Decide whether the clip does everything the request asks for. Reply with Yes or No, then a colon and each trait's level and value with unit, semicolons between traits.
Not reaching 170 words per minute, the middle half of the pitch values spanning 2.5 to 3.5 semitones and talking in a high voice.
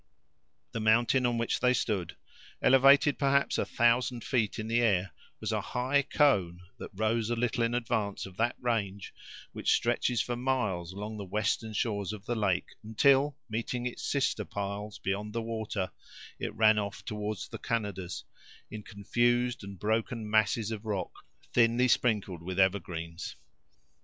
No: average, 155 wpm; average, 3.0 semitones; low, 110 Hz